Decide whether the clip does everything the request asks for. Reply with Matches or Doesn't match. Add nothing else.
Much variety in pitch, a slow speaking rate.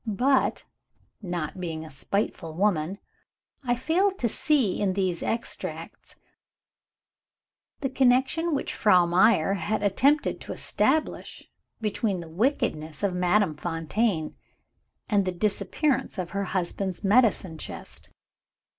Matches